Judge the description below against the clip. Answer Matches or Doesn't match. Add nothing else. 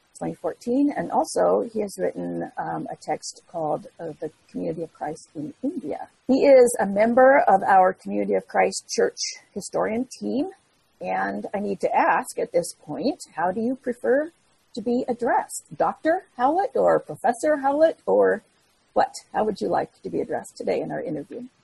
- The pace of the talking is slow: Doesn't match